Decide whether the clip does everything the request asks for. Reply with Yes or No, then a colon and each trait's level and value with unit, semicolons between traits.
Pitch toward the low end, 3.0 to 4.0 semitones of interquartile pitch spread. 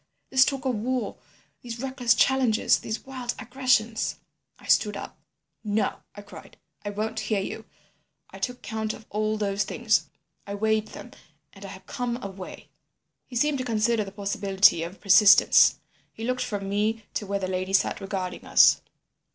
No: high, 215 Hz; average, 3.3 semitones